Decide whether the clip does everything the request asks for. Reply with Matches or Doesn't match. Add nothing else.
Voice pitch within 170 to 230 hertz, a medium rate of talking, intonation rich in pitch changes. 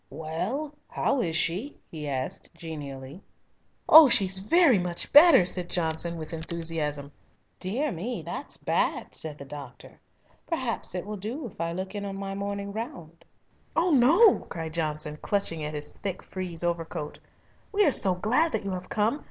Matches